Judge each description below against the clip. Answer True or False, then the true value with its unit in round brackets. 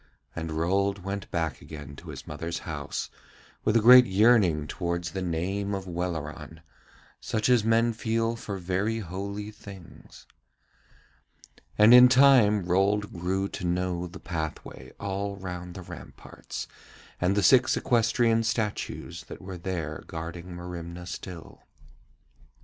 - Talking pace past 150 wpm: False (135 wpm)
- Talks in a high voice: False (95 Hz)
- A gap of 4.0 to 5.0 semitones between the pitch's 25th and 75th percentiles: False (3.6 semitones)